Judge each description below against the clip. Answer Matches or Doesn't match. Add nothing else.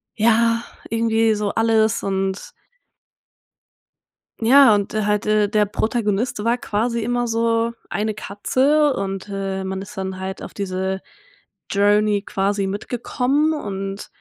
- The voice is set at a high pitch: Matches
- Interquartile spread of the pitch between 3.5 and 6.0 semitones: Doesn't match